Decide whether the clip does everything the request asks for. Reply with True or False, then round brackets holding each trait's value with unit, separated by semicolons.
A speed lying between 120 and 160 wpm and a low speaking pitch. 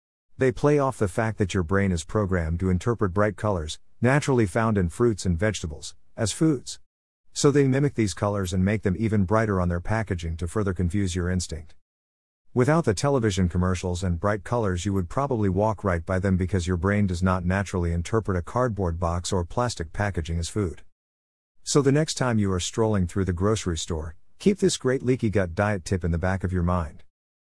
False (205 wpm; 95 Hz)